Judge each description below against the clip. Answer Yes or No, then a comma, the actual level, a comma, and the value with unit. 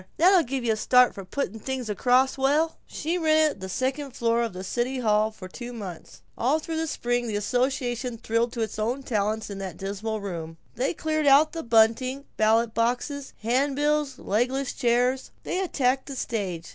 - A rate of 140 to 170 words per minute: No, average, 185 wpm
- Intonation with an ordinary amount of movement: Yes, average, 4.0 semitones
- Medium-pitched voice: No, high, 245 Hz